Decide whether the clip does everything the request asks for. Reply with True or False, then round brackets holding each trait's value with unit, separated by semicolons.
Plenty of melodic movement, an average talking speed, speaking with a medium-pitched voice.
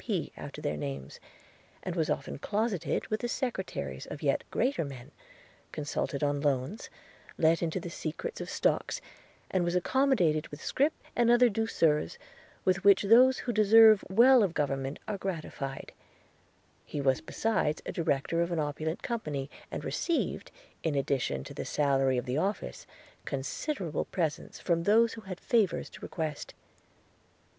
True (7.2 semitones; 150 wpm; 170 Hz)